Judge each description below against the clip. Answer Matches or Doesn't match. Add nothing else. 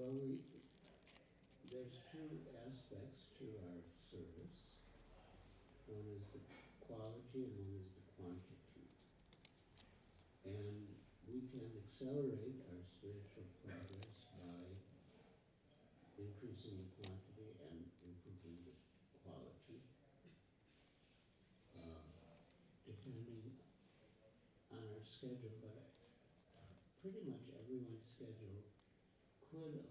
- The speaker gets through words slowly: Matches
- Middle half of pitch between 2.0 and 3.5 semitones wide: Doesn't match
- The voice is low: Matches